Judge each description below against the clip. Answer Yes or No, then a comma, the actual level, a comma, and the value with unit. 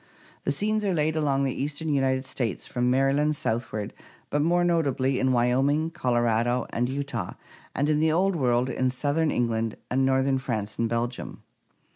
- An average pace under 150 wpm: No, average, 165 wpm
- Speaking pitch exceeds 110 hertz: Yes, low, 135 Hz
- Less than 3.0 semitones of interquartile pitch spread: No, average, 3.5 semitones